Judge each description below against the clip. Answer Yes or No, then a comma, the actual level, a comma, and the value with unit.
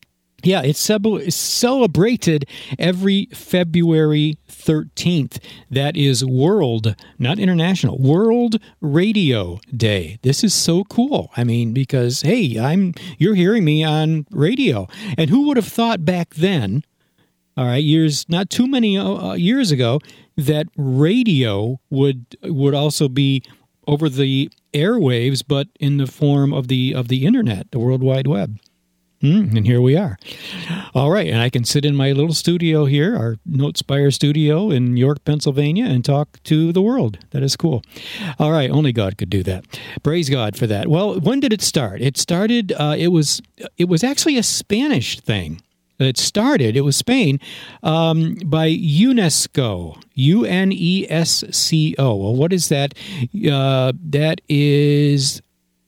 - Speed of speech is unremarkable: Yes, average, 150 wpm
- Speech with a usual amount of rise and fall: Yes, average, 5.0 semitones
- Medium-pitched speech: Yes, medium, 150 Hz